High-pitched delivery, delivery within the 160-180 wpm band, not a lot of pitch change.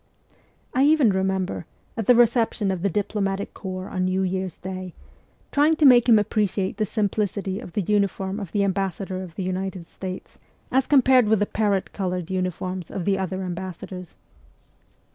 Yes: high, 195 Hz; average, 175 wpm; narrow, 2.3 semitones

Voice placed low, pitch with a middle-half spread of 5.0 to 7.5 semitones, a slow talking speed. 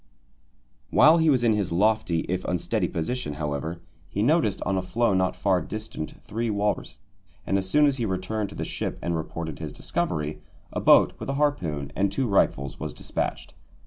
No: very low, 95 Hz; wide, 5.5 semitones; average, 185 wpm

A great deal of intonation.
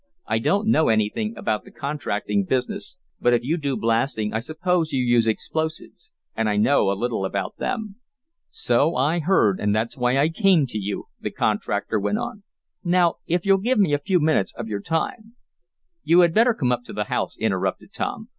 Yes: wide, 8.2 semitones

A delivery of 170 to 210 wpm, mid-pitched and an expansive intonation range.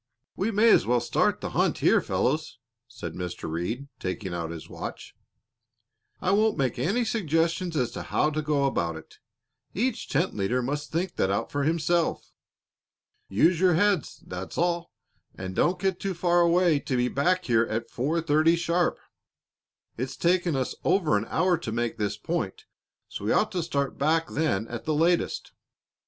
Yes: average, 175 wpm; medium, 155 Hz; wide, 6.7 semitones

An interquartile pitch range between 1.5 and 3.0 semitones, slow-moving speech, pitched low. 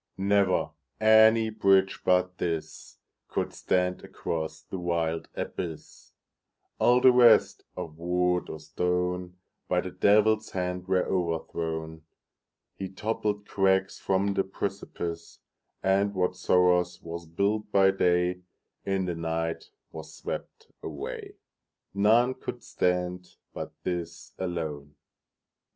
Yes: average, 2.7 semitones; slow, 95 wpm; very low, 90 Hz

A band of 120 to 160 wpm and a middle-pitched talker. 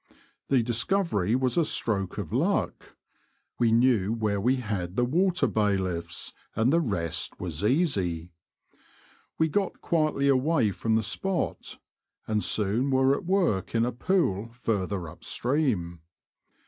No: average, 140 wpm; low, 115 Hz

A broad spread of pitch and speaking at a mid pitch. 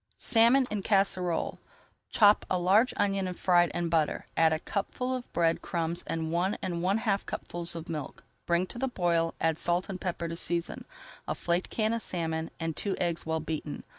No: average, 3.1 semitones; medium, 175 Hz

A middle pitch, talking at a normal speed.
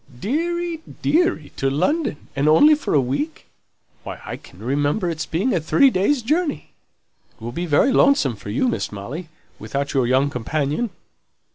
Yes: medium, 155 Hz; average, 160 wpm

